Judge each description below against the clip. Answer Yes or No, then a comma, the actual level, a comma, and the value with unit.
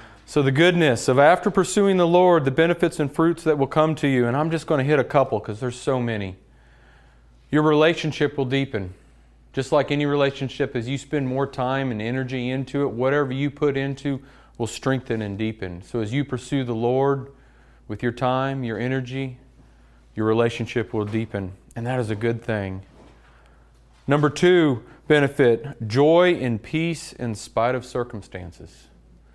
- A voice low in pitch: Yes, low, 130 Hz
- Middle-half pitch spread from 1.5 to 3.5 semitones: No, average, 4.6 semitones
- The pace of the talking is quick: No, average, 175 wpm